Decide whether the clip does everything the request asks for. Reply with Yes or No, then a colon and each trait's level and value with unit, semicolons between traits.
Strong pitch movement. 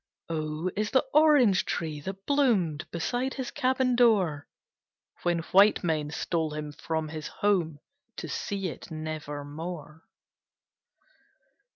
Yes: wide, 5.7 semitones